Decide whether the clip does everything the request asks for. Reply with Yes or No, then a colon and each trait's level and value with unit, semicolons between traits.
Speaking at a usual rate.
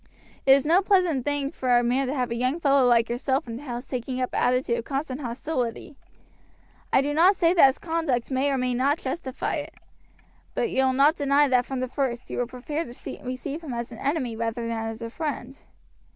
No: fast, 225 wpm